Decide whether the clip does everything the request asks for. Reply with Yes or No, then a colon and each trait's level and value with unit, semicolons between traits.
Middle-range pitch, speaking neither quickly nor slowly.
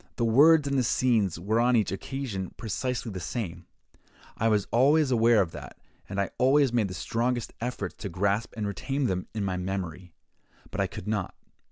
No: low, 110 Hz; average, 190 wpm